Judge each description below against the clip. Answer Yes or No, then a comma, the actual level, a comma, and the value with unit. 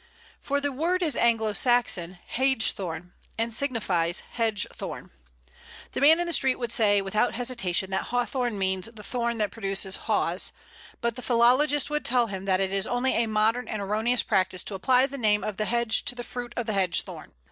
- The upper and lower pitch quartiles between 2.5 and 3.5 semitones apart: No, average, 4.0 semitones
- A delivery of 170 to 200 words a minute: Yes, average, 195 wpm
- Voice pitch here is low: No, high, 230 Hz